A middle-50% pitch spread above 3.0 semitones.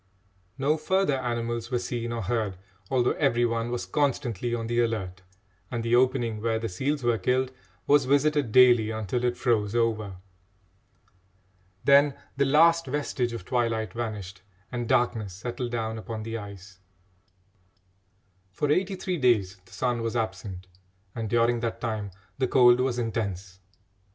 No: average, 2.7 semitones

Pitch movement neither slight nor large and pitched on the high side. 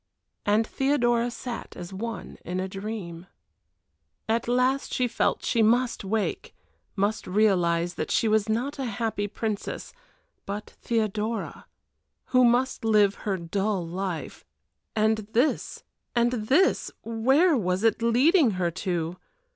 Yes: average, 3.7 semitones; high, 220 Hz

